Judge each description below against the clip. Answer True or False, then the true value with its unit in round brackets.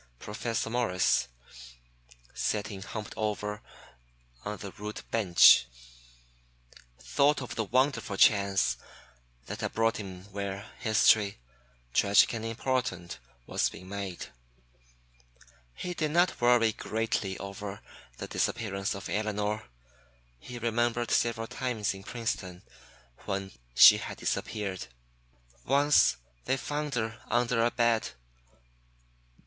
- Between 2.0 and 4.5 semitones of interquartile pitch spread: True (3.1 semitones)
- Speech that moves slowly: True (110 wpm)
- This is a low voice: True (110 Hz)